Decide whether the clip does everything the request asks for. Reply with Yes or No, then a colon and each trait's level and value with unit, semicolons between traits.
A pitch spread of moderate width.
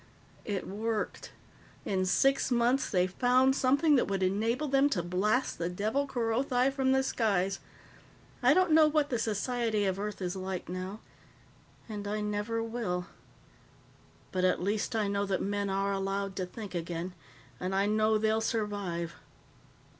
Yes: average, 4.1 semitones